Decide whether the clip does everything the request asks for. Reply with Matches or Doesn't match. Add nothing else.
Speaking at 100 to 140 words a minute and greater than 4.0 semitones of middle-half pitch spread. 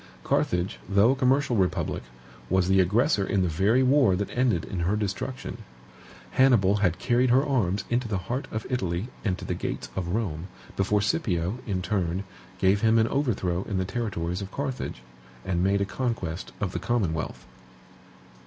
Doesn't match